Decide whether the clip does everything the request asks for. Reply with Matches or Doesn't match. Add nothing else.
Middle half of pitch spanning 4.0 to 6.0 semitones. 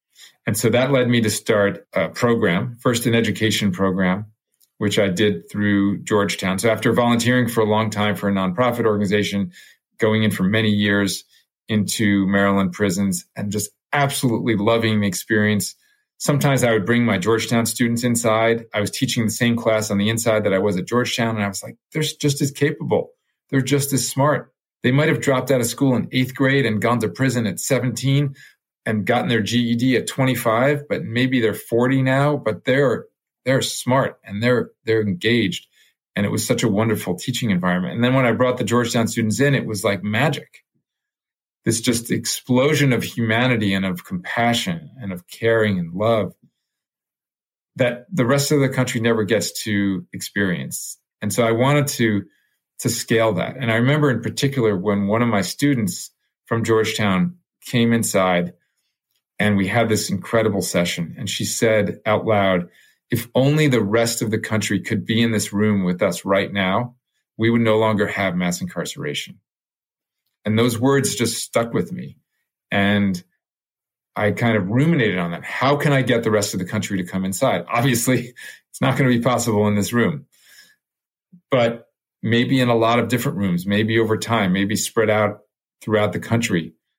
Doesn't match